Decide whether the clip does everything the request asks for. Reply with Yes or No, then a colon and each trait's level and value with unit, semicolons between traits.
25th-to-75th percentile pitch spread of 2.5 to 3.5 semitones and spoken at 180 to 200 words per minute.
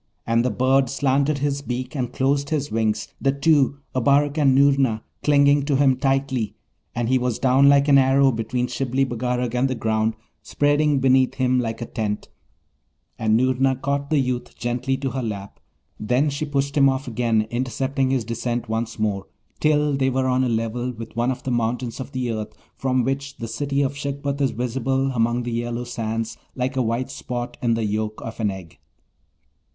Yes: average, 2.9 semitones; average, 190 wpm